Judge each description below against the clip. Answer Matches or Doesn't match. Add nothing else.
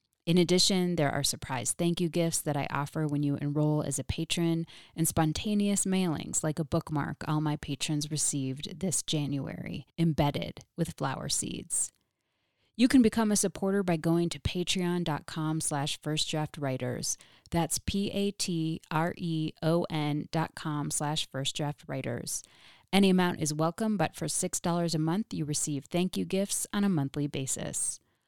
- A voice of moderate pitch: Matches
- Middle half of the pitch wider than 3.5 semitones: Doesn't match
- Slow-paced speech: Doesn't match